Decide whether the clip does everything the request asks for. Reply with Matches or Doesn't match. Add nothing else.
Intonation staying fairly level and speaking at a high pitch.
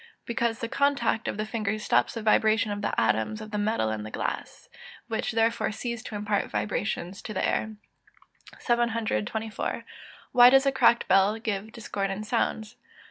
Matches